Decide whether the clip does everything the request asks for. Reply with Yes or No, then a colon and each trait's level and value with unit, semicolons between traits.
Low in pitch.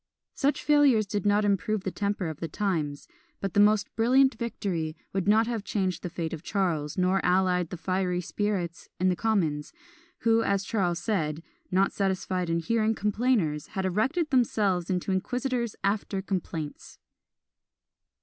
No: high, 195 Hz